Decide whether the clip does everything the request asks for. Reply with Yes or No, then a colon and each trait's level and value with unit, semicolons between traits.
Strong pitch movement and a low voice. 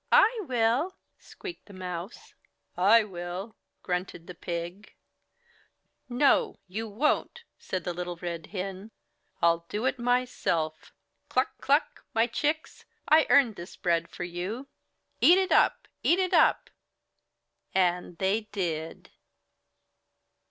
No: wide, 5.9 semitones; high, 195 Hz